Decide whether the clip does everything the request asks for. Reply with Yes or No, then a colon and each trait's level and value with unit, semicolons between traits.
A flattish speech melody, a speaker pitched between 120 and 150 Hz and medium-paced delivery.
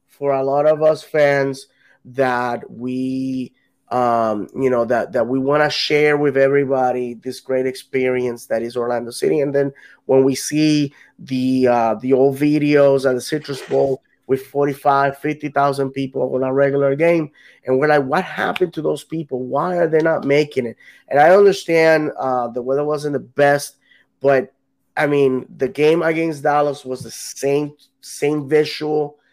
Yes: narrow, 2.3 semitones; medium, 140 Hz; average, 170 wpm